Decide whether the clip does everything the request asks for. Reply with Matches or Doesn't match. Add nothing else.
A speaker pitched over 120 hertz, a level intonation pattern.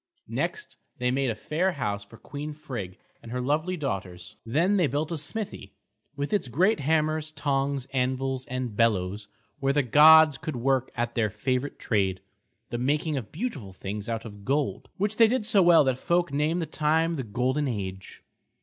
Doesn't match